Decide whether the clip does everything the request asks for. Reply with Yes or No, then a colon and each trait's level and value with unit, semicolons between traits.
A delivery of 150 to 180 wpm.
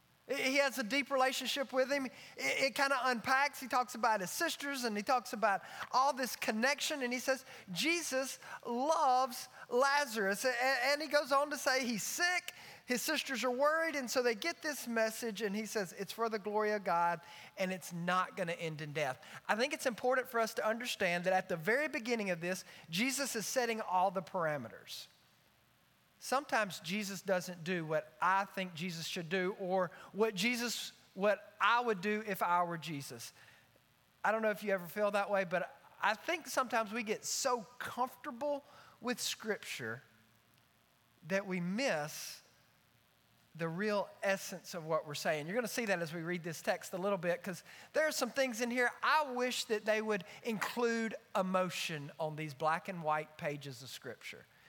No: average, 190 wpm